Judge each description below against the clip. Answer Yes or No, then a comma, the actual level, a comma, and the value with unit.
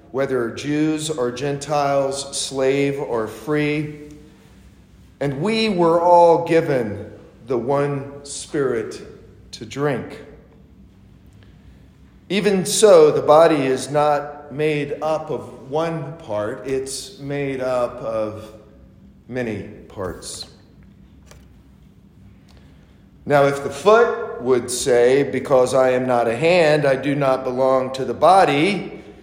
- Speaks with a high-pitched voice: No, medium, 140 Hz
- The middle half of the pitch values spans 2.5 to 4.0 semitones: Yes, average, 3.4 semitones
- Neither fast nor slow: No, slow, 110 wpm